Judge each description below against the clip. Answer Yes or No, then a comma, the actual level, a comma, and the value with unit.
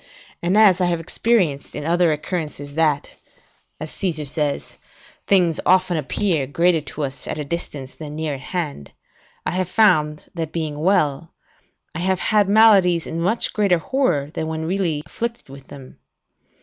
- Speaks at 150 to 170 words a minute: Yes, average, 160 wpm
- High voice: No, medium, 165 Hz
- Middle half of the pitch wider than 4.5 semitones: No, average, 3.7 semitones